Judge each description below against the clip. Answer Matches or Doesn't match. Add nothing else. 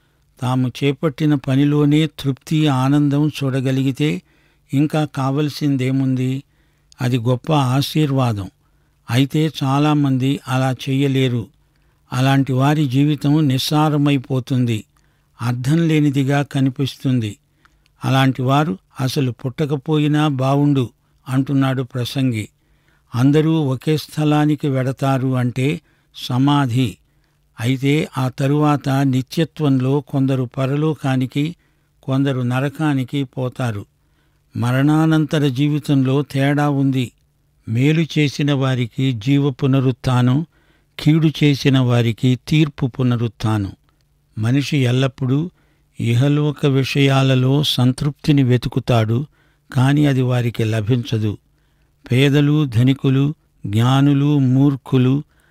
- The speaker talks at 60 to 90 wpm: Matches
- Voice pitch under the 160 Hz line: Matches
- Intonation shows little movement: Matches